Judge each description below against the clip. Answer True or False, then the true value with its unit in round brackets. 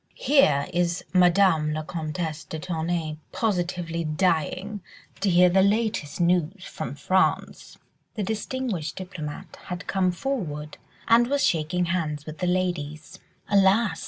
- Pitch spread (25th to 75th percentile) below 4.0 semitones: True (3.6 semitones)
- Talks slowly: True (130 wpm)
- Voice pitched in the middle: True (180 Hz)